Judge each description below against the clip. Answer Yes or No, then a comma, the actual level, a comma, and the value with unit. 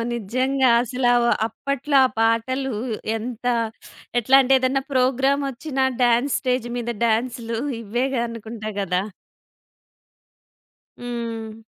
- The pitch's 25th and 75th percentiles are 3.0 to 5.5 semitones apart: No, narrow, 2.6 semitones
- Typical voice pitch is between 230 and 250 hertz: Yes, high, 245 Hz